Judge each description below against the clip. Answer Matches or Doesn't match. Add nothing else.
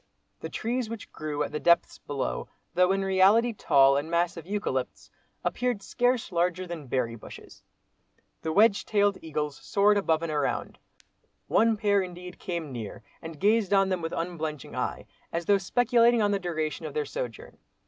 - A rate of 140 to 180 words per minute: Matches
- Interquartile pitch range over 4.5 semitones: Matches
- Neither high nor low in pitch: Matches